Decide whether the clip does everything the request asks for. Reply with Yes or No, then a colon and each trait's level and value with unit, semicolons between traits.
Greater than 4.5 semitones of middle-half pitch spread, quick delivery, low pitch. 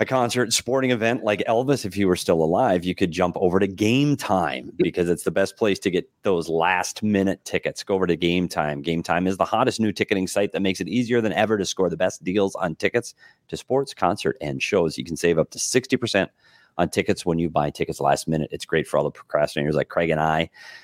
Yes: average, 5.1 semitones; fast, 240 wpm; very low, 95 Hz